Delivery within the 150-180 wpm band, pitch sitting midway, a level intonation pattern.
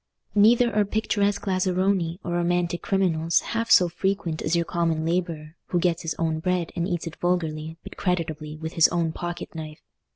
Yes: average, 175 wpm; medium, 175 Hz; narrow, 2.3 semitones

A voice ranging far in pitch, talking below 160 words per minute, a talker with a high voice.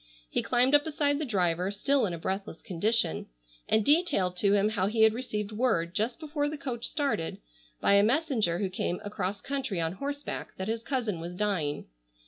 No: wide, 6.4 semitones; average, 190 wpm; high, 215 Hz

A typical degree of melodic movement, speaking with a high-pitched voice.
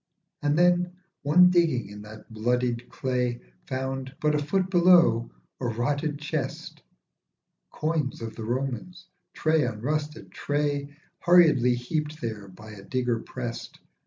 No: average, 4.3 semitones; low, 135 Hz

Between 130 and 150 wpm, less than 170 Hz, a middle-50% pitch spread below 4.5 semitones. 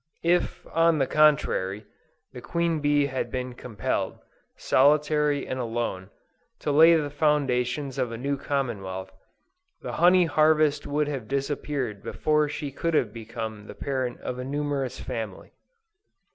Yes: average, 140 wpm; medium, 140 Hz; average, 3.5 semitones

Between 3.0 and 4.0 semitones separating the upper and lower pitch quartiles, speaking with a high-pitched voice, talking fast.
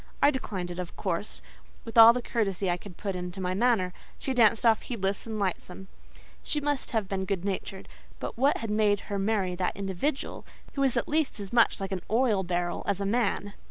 Yes: average, 3.7 semitones; high, 200 Hz; fast, 210 wpm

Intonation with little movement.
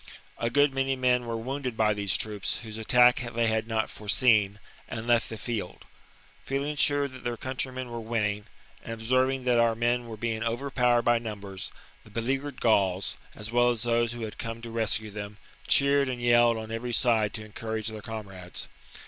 Yes: narrow, 2.1 semitones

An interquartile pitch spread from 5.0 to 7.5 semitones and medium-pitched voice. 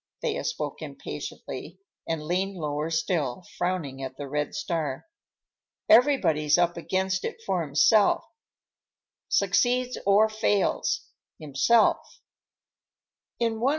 Yes: average, 5.3 semitones; medium, 175 Hz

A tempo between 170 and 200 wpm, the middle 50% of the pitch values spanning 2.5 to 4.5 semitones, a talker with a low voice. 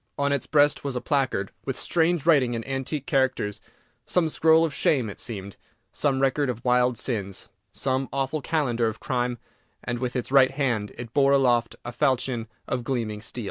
Yes: average, 180 wpm; average, 2.9 semitones; low, 130 Hz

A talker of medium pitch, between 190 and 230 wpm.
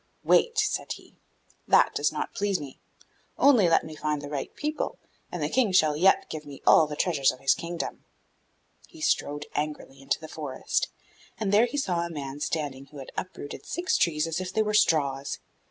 Yes: medium, 155 Hz; average, 195 wpm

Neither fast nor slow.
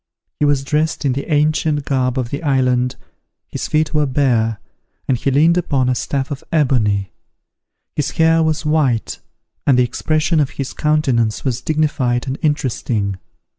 Yes: average, 160 wpm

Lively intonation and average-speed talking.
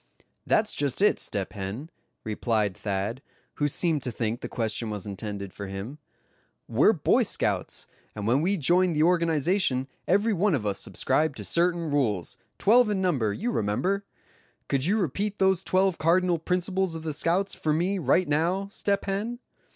Yes: wide, 8.7 semitones; average, 165 wpm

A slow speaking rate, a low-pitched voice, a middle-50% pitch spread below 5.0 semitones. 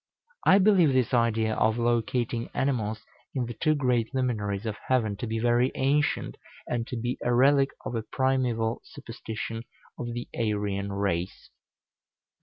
No: average, 150 wpm; low, 120 Hz; average, 2.8 semitones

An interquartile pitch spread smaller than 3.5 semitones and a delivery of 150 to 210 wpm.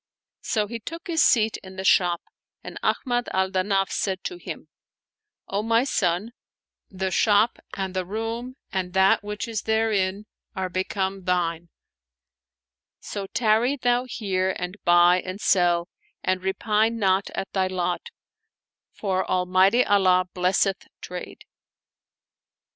No: average, 3.1 semitones; slow, 135 wpm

